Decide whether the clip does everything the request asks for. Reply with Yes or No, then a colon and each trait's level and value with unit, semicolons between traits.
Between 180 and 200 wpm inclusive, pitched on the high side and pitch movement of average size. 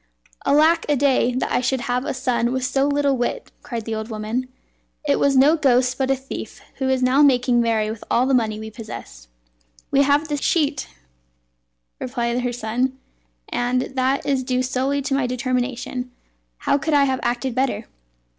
No: average, 185 wpm; very high, 255 Hz; narrow, 2.2 semitones